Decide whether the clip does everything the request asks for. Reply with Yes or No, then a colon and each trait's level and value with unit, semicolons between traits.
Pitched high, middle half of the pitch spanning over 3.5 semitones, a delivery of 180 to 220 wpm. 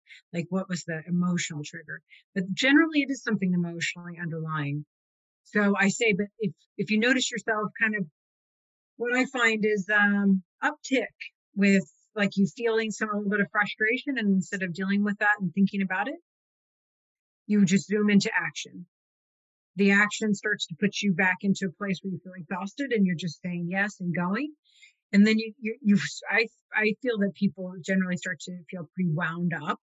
No: high, 200 Hz; average, 3.0 semitones; average, 185 wpm